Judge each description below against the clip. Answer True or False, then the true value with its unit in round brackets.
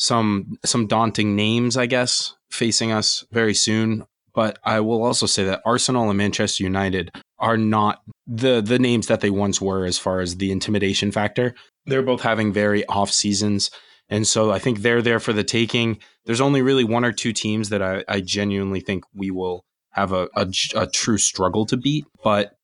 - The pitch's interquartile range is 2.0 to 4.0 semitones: True (2.8 semitones)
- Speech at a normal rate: True (195 wpm)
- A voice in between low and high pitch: False (110 Hz)